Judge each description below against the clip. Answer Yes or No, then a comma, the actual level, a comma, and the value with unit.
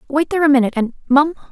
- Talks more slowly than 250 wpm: Yes, average, 200 wpm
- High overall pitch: Yes, very high, 280 Hz